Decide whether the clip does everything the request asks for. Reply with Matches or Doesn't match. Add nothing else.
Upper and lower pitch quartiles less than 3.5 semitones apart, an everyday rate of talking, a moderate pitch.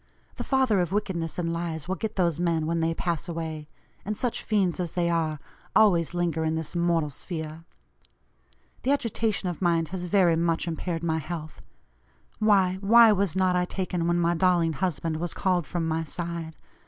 Matches